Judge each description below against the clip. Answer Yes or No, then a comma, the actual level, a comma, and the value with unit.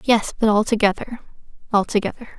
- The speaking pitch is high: Yes, high, 215 Hz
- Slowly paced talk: Yes, slow, 100 wpm